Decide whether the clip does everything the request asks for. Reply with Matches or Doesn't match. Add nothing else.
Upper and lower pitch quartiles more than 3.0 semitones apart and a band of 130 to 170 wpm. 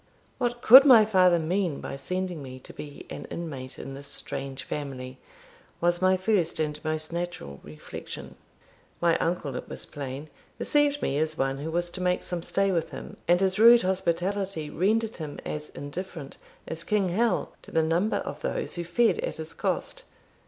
Doesn't match